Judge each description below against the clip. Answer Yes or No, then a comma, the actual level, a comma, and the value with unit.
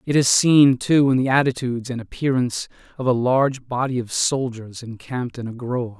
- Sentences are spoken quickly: No, average, 190 wpm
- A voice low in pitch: Yes, low, 125 Hz